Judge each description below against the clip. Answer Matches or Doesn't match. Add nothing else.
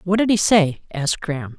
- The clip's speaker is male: Matches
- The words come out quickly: Matches